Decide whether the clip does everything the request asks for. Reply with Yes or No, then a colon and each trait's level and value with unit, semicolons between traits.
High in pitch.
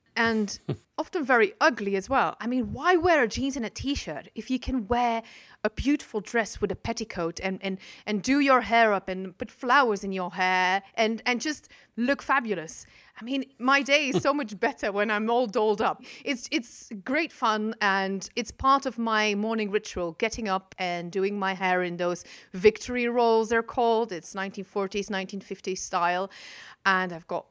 Yes: high, 220 Hz